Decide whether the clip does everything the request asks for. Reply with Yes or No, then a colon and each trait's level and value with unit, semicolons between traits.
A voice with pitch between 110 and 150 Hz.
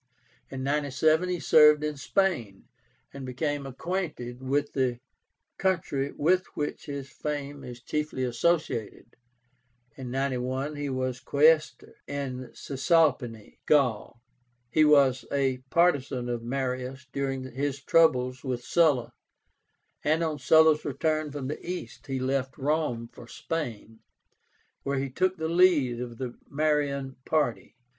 Yes: medium, 140 Hz